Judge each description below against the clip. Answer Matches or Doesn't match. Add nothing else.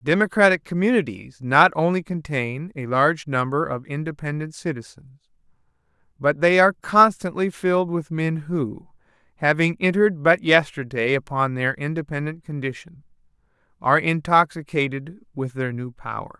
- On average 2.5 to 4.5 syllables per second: Doesn't match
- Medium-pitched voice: Matches